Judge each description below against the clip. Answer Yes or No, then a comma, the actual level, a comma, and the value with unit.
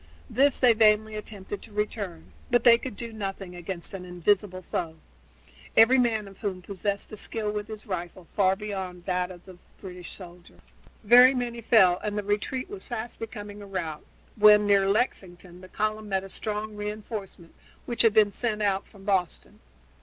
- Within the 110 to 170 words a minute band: No, average, 180 wpm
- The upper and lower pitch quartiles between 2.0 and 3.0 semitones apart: Yes, average, 2.7 semitones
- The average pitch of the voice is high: Yes, high, 205 Hz